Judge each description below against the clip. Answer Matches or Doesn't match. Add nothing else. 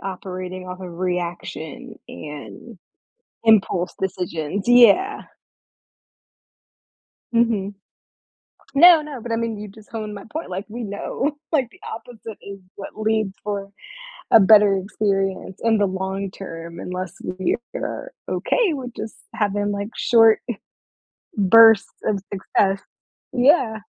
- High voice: Matches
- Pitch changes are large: Doesn't match